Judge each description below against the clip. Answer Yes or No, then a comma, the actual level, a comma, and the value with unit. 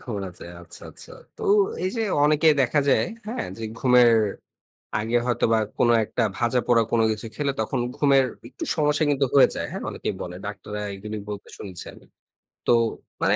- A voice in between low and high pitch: No, low, 120 Hz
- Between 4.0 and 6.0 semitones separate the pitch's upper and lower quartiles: Yes, average, 4.7 semitones